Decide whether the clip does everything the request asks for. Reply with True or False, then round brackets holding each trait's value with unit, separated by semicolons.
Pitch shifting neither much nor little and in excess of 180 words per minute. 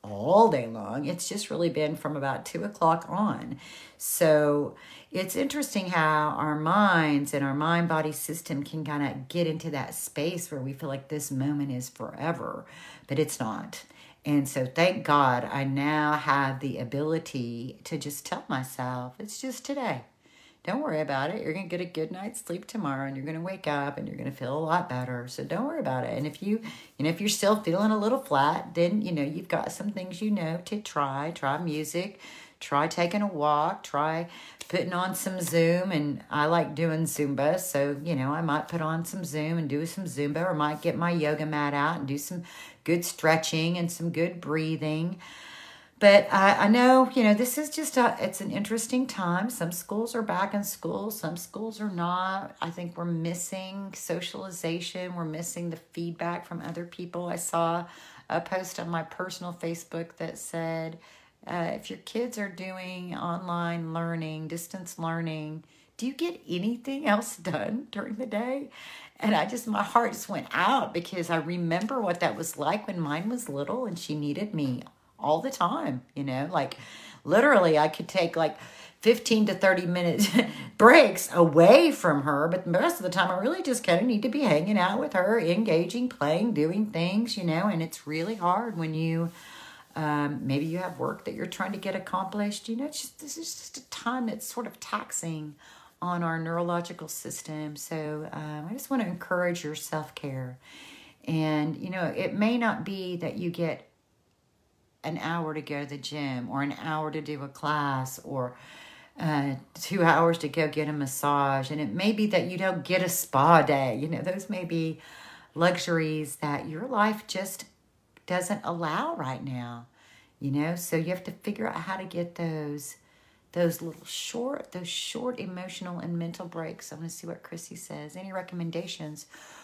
True (4.0 semitones; 195 wpm)